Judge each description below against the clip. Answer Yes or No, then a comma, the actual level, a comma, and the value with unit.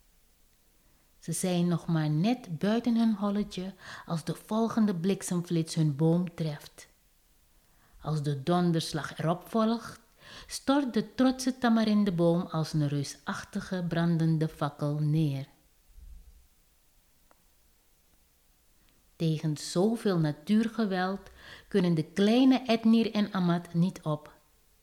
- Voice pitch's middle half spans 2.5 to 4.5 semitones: No, wide, 5.5 semitones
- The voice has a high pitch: No, medium, 165 Hz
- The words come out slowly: Yes, slow, 100 wpm